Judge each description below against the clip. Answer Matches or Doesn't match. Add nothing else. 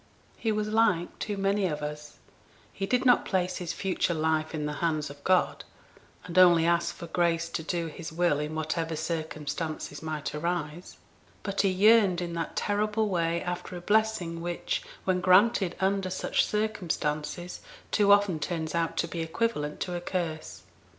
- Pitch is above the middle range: Doesn't match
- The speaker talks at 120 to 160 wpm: Doesn't match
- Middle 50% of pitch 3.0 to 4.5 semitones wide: Matches